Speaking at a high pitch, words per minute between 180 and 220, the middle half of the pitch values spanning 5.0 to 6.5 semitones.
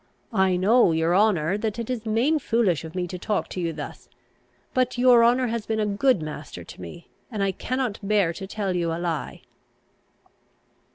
Yes: high, 205 Hz; average, 190 wpm; average, 5.3 semitones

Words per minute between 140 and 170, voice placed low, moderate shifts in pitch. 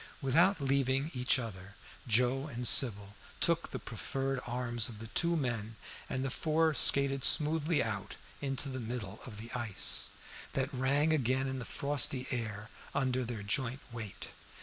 Yes: average, 155 wpm; low, 130 Hz; average, 3.2 semitones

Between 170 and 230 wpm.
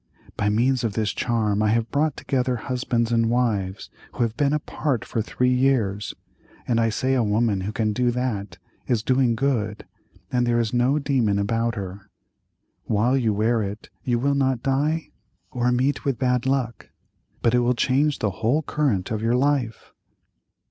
Yes: average, 175 wpm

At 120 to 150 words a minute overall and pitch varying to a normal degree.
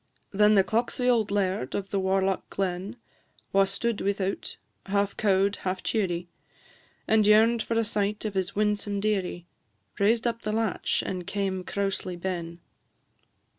No: average, 145 wpm; narrow, 2.0 semitones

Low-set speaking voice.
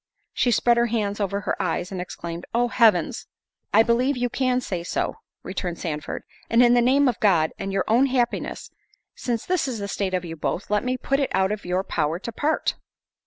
No: high, 215 Hz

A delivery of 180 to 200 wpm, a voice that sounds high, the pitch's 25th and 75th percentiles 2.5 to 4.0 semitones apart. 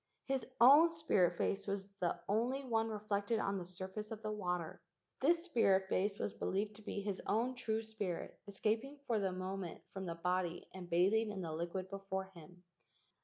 Yes: average, 185 wpm; high, 200 Hz; average, 3.2 semitones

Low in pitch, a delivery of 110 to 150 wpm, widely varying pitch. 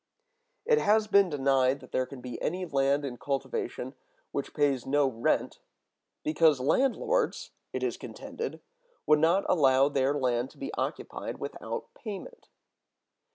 No: medium, 145 Hz; average, 140 wpm; wide, 7.0 semitones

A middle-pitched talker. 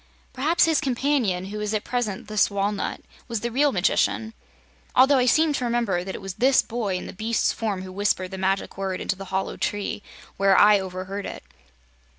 No: high, 210 Hz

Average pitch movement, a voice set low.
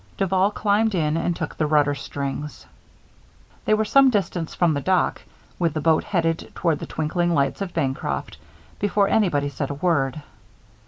No: average, 4.8 semitones; medium, 165 Hz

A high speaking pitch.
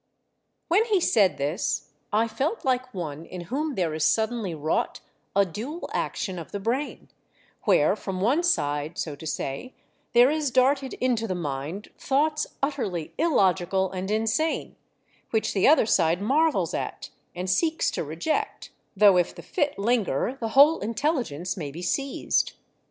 Yes: high, 215 Hz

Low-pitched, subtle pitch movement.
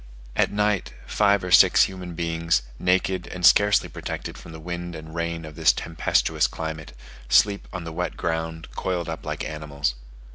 Yes: very low, 85 Hz; narrow, 2.2 semitones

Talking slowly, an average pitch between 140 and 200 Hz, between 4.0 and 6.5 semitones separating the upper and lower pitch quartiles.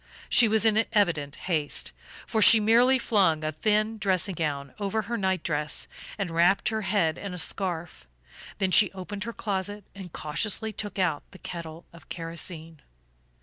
No: average, 165 wpm; high, 190 Hz; average, 4.3 semitones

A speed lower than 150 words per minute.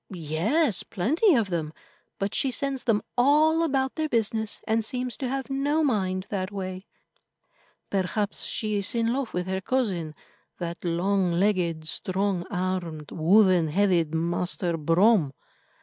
Yes: average, 140 wpm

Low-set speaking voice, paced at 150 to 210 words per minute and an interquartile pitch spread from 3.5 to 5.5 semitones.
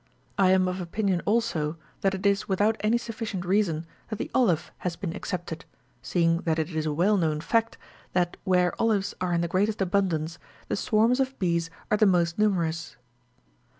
No: medium, 185 Hz; average, 185 wpm; average, 3.8 semitones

